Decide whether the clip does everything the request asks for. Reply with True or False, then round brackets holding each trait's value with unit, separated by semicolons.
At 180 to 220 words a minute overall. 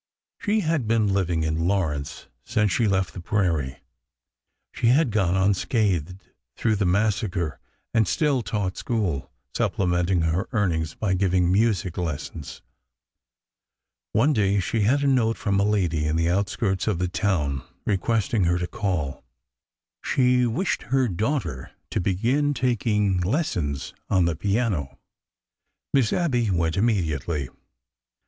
False (135 wpm)